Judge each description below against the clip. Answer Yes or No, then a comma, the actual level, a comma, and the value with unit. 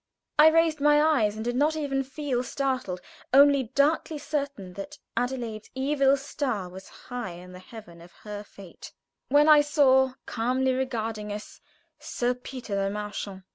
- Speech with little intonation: No, wide, 5.4 semitones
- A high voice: Yes, very high, 255 Hz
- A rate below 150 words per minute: No, average, 155 wpm